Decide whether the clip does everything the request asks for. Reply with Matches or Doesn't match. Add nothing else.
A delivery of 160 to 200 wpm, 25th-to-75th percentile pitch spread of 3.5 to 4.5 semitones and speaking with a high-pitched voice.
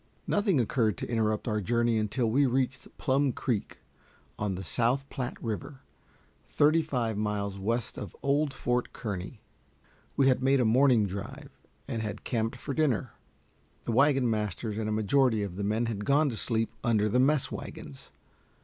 Doesn't match